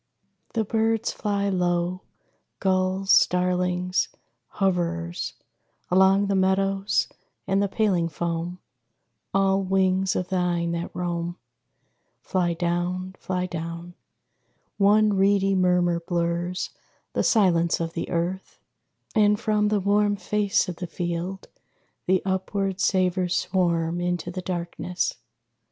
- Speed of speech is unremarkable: No, slow, 110 wpm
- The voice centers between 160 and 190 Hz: Yes, medium, 185 Hz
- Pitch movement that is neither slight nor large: No, narrow, 2.0 semitones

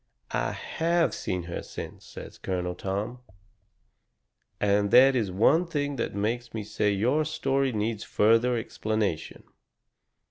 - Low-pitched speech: Yes, low, 110 Hz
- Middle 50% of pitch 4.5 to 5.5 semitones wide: Yes, average, 4.8 semitones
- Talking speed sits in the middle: No, slow, 130 wpm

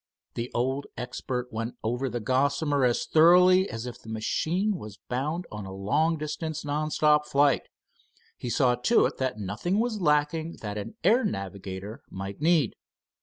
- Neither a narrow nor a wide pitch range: No, wide, 5.9 semitones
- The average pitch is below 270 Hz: Yes, low, 135 Hz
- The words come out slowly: No, average, 165 wpm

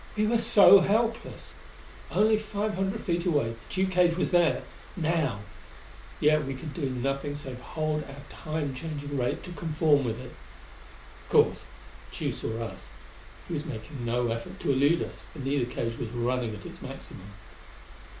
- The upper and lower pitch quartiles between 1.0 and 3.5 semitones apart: No, wide, 5.5 semitones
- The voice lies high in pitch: No, medium, 145 Hz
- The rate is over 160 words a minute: Yes, average, 170 wpm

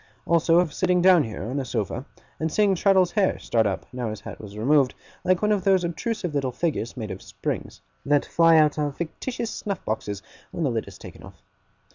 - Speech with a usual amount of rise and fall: No, wide, 7.4 semitones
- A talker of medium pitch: Yes, medium, 155 Hz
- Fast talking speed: Yes, fast, 210 wpm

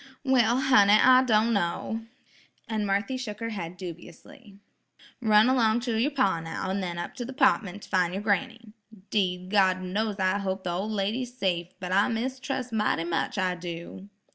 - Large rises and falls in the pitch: No, average, 4.1 semitones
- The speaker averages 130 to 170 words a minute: No, average, 180 wpm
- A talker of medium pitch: No, high, 210 Hz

